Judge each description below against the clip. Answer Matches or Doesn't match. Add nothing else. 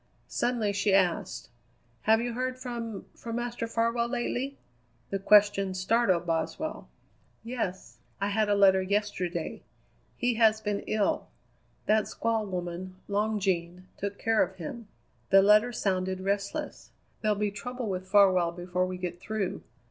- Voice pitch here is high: Matches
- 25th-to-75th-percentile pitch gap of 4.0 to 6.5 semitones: Doesn't match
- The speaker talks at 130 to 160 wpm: Matches